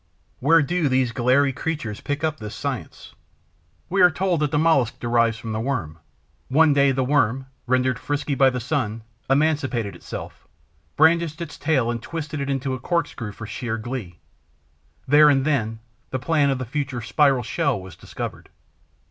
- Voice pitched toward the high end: No, low, 135 Hz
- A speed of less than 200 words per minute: Yes, average, 170 wpm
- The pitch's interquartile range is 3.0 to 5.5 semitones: Yes, average, 4.2 semitones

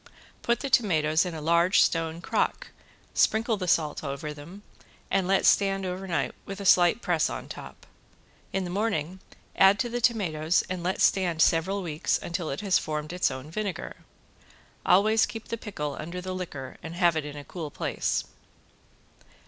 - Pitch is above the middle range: No, medium, 180 Hz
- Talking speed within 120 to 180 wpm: Yes, average, 175 wpm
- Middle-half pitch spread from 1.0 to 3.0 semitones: No, average, 3.7 semitones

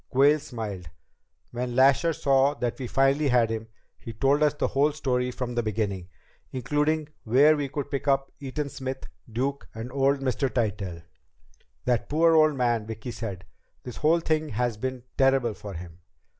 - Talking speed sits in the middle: Yes, average, 170 wpm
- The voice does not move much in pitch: No, average, 3.8 semitones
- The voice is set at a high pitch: No, low, 130 Hz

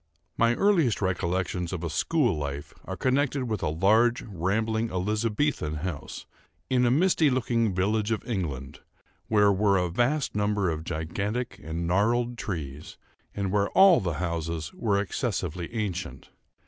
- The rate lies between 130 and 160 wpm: Yes, average, 145 wpm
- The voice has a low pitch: Yes, low, 100 Hz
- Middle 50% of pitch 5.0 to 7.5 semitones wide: Yes, wide, 5.4 semitones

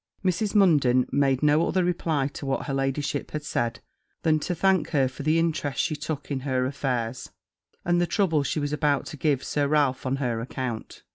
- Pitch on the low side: No, medium, 145 Hz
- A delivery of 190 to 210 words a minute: Yes, average, 200 wpm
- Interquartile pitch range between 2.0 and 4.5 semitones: Yes, average, 3.0 semitones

